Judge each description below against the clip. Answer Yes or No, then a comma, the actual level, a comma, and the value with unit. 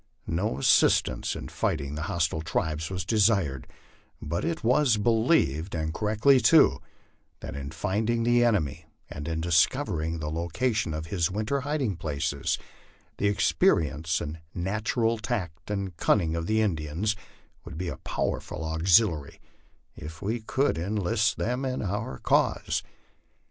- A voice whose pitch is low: Yes, very low, 90 Hz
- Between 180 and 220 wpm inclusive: No, average, 145 wpm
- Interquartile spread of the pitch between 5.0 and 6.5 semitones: Yes, wide, 5.6 semitones